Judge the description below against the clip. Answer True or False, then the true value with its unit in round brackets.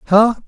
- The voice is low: False (215 Hz)